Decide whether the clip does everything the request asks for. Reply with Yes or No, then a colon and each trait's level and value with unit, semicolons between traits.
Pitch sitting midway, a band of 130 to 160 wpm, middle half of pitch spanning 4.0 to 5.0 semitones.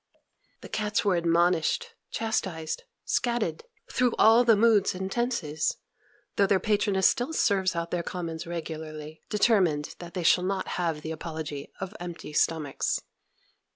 Yes: medium, 180 Hz; average, 145 wpm; average, 4.5 semitones